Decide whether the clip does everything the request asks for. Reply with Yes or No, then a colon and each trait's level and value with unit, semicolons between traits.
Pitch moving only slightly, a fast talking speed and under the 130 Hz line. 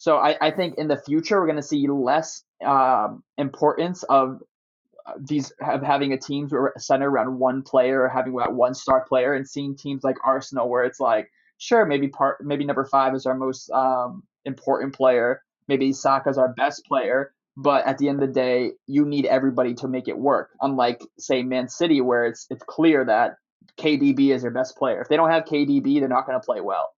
No: narrow, 1.9 semitones; fast, 210 wpm; low, 135 Hz